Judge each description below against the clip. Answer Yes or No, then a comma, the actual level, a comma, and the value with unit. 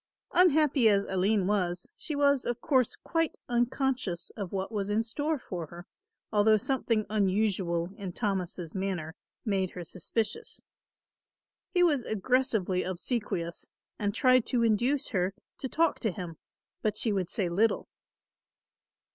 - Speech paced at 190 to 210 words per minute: No, average, 140 wpm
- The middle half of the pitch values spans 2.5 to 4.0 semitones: No, average, 5.3 semitones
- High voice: Yes, high, 210 Hz